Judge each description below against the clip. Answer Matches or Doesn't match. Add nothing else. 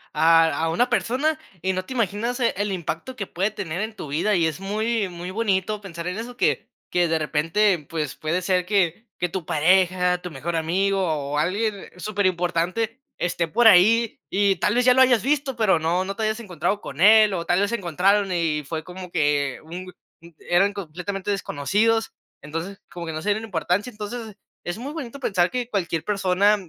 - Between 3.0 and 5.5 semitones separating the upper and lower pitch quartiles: Matches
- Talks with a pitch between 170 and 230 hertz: Matches